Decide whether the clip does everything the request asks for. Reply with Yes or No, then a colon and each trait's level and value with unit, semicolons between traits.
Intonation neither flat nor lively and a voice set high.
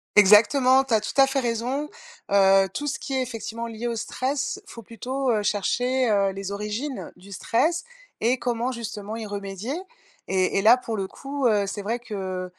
Yes: average, 4.0 semitones; high, 230 Hz